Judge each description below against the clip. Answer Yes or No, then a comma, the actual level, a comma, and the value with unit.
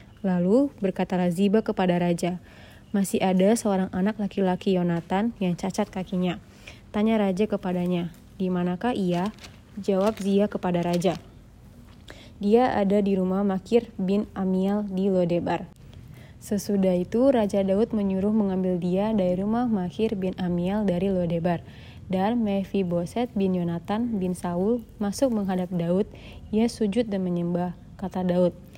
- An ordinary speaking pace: Yes, average, 130 wpm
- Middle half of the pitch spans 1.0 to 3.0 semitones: Yes, narrow, 2.6 semitones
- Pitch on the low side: No, high, 190 Hz